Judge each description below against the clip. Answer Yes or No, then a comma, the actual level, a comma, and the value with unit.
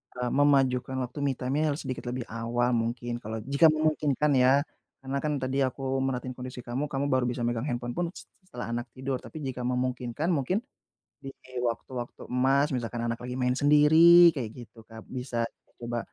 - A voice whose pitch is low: Yes, low, 130 Hz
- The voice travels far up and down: No, narrow, 2.6 semitones